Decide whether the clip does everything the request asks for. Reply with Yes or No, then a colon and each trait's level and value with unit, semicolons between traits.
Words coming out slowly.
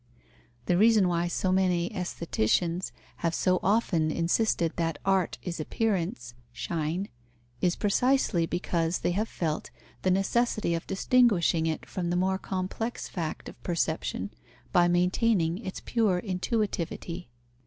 Yes: slow, 130 wpm